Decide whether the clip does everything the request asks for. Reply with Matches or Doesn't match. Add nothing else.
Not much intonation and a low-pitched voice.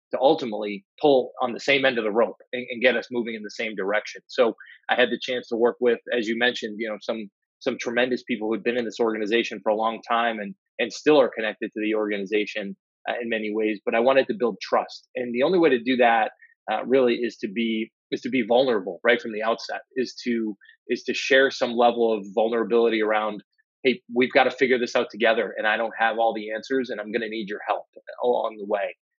Matches